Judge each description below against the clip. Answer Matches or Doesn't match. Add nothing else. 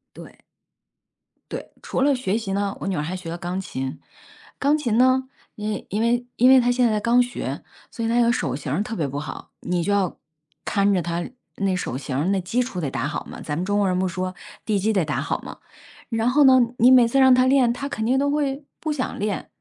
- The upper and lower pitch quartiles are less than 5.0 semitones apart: Doesn't match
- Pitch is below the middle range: Doesn't match